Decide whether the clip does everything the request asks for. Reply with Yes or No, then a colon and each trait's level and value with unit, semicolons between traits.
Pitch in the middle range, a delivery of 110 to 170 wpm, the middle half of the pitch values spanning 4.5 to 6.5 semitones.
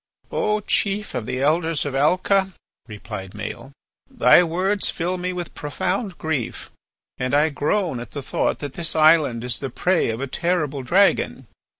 Yes: medium, 155 Hz; average, 165 wpm; wide, 5.5 semitones